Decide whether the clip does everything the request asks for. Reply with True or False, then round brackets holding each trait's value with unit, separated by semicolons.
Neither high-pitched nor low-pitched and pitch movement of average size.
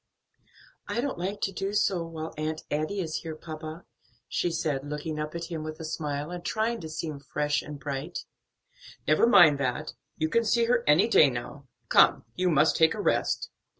True (160 Hz; 3.4 semitones)